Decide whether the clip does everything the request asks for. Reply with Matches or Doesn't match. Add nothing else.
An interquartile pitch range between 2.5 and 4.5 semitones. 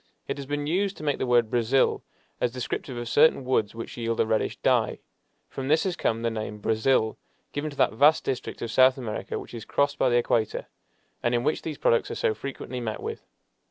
Matches